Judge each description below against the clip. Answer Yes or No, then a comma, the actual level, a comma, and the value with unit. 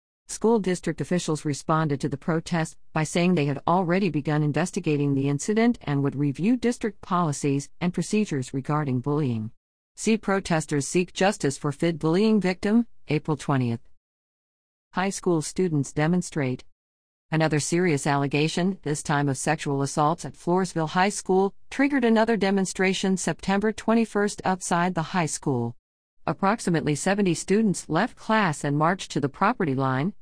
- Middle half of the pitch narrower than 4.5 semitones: No, average, 4.8 semitones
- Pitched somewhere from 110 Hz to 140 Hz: No, medium, 160 Hz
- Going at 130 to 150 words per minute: Yes, average, 140 wpm